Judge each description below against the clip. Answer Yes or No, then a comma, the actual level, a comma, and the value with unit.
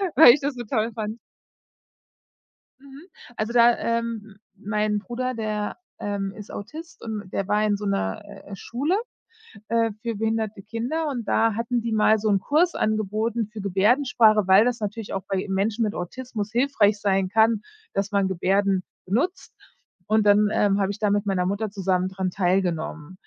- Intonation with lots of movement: No, average, 2.8 semitones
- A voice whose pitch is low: No, high, 210 Hz